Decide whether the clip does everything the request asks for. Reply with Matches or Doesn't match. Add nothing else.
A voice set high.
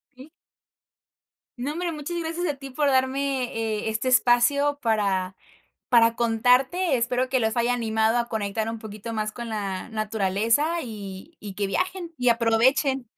Matches